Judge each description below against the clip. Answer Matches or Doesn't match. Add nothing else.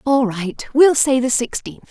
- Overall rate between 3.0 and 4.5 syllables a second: Matches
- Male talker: Doesn't match